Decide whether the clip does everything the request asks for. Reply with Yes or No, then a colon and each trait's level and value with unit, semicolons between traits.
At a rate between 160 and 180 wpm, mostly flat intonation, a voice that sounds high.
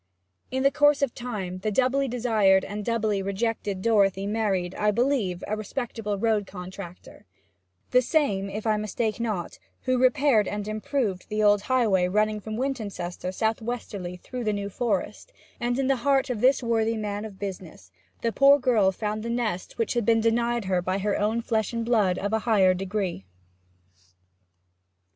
No: average, 170 wpm; average, 3.4 semitones; high, 215 Hz